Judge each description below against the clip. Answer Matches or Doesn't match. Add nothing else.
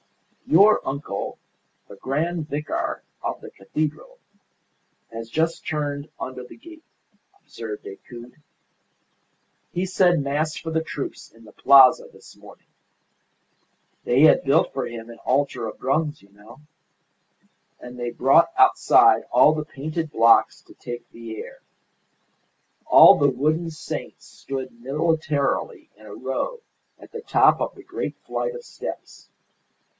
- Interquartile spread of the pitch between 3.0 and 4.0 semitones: Doesn't match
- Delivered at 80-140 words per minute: Matches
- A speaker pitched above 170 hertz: Doesn't match